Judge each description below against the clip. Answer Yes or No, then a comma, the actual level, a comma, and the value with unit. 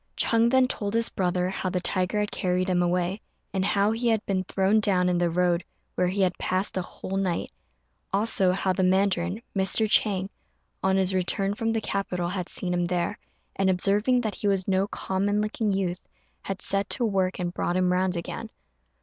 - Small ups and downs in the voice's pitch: Yes, narrow, 2.1 semitones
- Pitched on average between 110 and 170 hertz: No, high, 190 Hz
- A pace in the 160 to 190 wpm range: No, average, 200 wpm